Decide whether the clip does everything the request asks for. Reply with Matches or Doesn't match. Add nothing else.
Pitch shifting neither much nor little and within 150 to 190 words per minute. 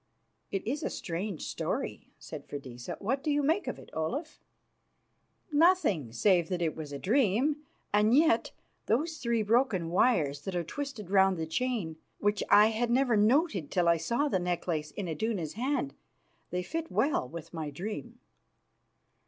Doesn't match